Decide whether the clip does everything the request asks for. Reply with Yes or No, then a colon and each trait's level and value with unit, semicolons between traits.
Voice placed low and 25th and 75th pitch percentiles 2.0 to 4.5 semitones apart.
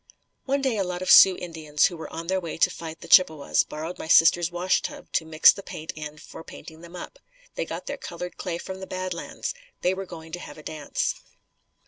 No: medium, 170 Hz; narrow, 2.5 semitones